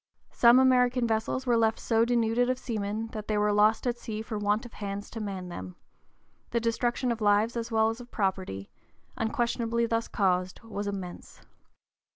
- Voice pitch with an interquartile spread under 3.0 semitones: Yes, narrow, 2.4 semitones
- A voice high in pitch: Yes, high, 225 Hz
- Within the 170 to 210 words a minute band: Yes, average, 175 wpm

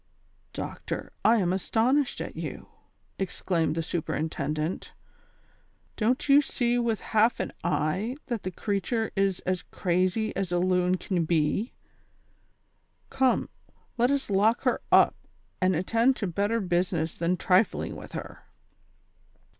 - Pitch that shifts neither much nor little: Yes, average, 4.6 semitones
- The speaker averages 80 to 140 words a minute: Yes, slow, 135 wpm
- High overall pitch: Yes, high, 195 Hz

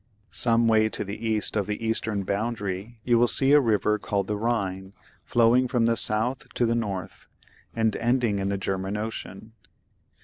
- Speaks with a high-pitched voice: No, low, 110 Hz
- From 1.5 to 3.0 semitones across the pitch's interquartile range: Yes, average, 2.7 semitones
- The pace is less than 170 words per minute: No, average, 175 wpm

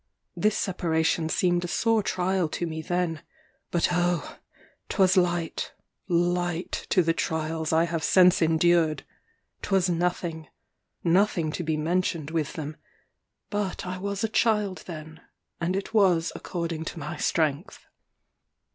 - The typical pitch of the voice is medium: Yes, medium, 175 Hz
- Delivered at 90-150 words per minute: Yes, slow, 135 wpm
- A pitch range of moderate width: No, narrow, 2.3 semitones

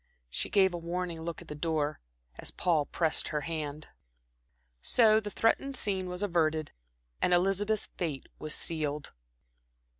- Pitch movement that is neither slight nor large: Yes, average, 3.7 semitones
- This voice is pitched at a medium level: Yes, medium, 170 Hz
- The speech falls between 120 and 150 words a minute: Yes, average, 145 wpm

